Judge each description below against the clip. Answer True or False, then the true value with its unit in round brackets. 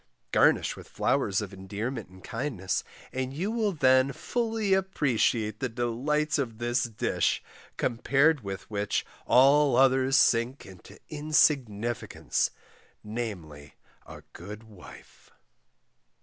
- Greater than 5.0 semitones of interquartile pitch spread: True (5.5 semitones)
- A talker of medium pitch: False (125 Hz)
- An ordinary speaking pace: False (110 wpm)